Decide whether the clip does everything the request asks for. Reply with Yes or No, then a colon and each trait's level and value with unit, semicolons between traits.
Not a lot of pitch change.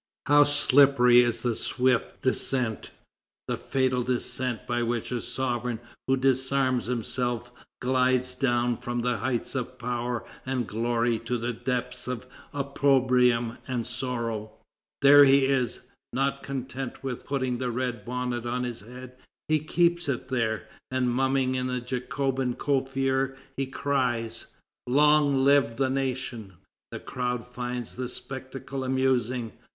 Yes: narrow, 1.7 semitones